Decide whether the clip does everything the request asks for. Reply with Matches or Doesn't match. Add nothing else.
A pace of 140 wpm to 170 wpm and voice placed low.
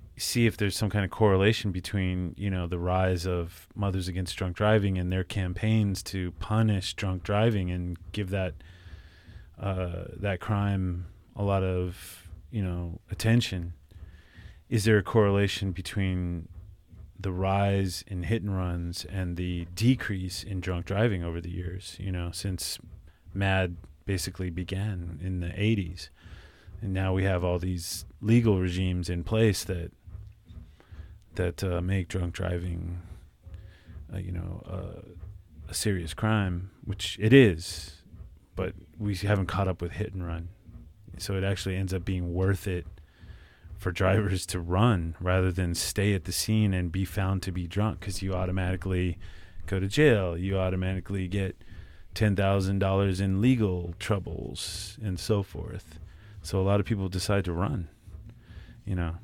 Matches